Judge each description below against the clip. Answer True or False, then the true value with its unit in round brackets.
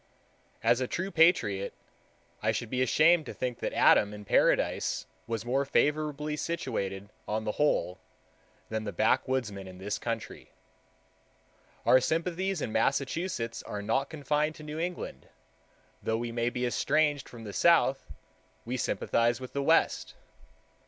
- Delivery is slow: False (145 wpm)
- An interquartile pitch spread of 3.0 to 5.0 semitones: False (5.6 semitones)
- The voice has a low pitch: True (130 Hz)